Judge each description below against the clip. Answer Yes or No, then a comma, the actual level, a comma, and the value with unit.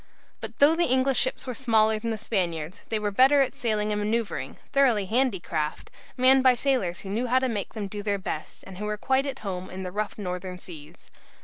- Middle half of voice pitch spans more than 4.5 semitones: Yes, average, 5.2 semitones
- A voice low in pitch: No, high, 215 Hz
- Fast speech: Yes, fast, 225 wpm